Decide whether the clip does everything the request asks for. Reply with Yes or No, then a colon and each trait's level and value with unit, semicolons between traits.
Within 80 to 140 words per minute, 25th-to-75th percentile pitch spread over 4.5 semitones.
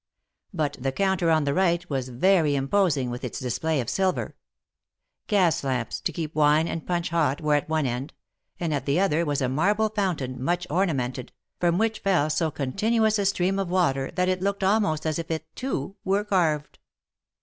No: average, 195 wpm; average, 5.1 semitones